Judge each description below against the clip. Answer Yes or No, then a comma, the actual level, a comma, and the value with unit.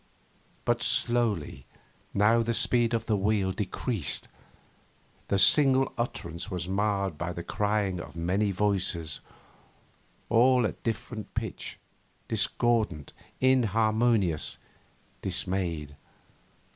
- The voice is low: Yes, low, 105 Hz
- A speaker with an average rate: No, slow, 95 wpm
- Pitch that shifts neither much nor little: Yes, average, 4.3 semitones